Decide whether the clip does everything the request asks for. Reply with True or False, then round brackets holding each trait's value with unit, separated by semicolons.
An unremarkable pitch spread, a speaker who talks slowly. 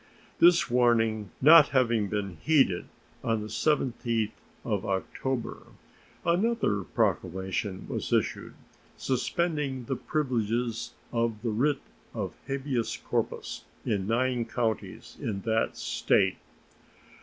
True (4.0 semitones; 105 wpm)